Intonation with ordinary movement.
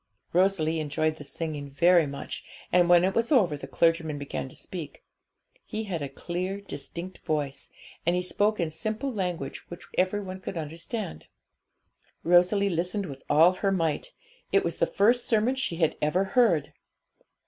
Yes: average, 3.9 semitones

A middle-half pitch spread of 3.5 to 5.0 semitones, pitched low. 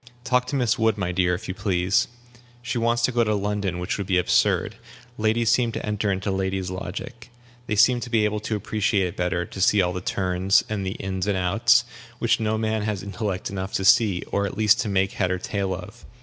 No: average, 2.9 semitones; low, 100 Hz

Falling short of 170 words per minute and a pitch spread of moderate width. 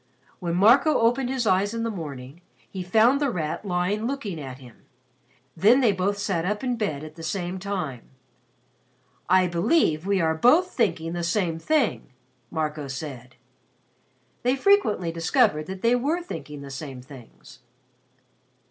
No: average, 155 wpm; wide, 6.8 semitones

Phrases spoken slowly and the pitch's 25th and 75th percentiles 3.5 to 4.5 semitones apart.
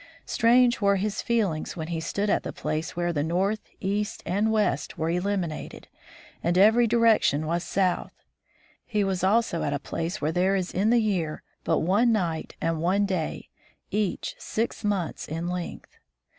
No: average, 165 wpm; average, 4.1 semitones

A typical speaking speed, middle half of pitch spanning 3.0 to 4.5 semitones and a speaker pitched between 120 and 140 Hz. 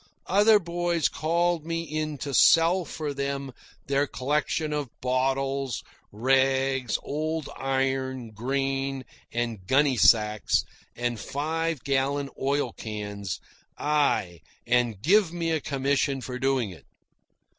No: slow, 115 wpm; average, 3.3 semitones; low, 135 Hz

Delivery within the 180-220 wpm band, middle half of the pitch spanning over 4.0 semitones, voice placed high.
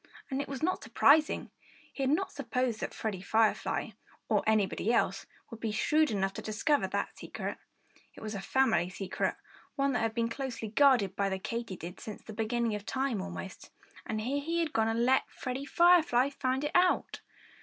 Yes: average, 185 wpm; average, 4.7 semitones; high, 235 Hz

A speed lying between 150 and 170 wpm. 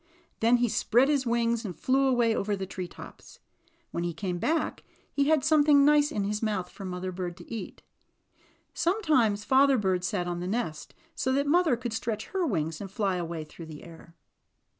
No: average, 195 wpm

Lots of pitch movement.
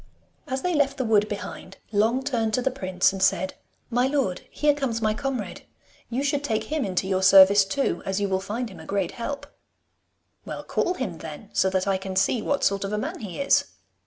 Yes: wide, 5.7 semitones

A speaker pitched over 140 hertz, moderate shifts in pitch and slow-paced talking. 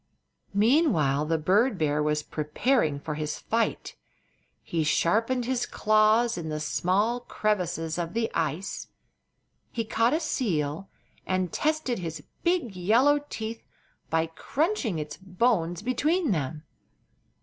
No: high, 190 Hz; wide, 7.3 semitones; slow, 125 wpm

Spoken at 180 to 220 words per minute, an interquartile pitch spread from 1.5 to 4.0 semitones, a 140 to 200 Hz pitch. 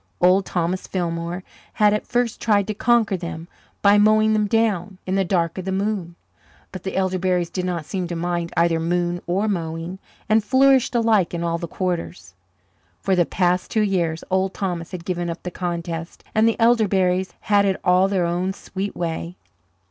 Yes: average, 185 wpm; average, 2.9 semitones; medium, 185 Hz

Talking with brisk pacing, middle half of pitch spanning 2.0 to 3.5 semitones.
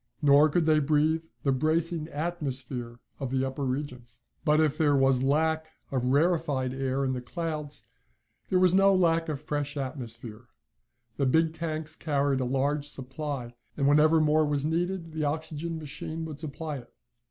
No: average, 165 wpm; average, 3.0 semitones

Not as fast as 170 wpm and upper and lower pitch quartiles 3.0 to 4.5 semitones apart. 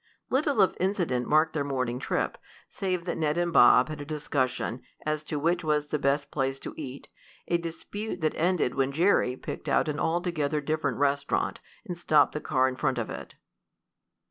No: average, 185 wpm; average, 3.8 semitones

